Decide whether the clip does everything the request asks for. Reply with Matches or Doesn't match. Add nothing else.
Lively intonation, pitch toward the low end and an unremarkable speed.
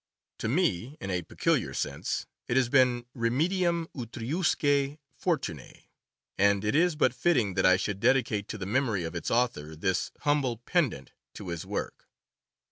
Matches